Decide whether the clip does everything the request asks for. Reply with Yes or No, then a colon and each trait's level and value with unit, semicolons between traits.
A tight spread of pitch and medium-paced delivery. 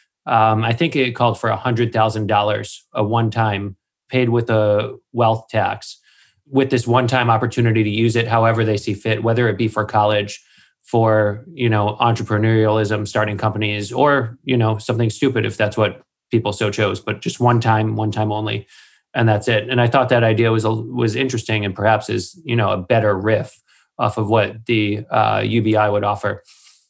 Yes: narrow, 1.9 semitones; average, 190 wpm